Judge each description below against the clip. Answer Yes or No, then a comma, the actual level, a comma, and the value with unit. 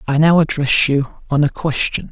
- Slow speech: No, average, 200 wpm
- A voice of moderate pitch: Yes, medium, 145 Hz